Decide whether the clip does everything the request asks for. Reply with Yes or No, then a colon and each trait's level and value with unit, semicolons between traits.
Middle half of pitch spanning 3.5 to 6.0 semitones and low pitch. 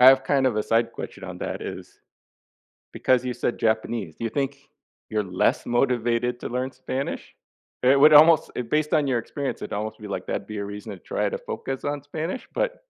Yes: average, 4.1 semitones; low, 125 Hz